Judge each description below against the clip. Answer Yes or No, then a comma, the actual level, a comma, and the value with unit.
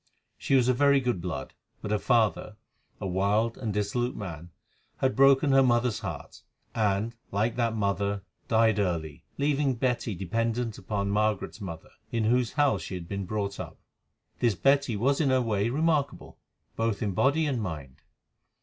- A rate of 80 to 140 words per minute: No, average, 165 wpm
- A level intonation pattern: No, average, 4.3 semitones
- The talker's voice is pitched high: No, low, 115 Hz